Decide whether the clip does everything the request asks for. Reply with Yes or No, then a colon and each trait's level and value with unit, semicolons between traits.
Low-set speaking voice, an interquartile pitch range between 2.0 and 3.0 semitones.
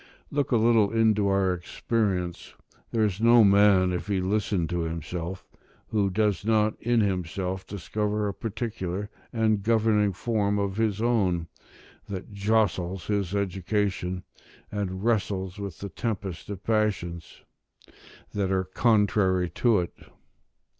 Yes: low, 100 Hz; average, 2.7 semitones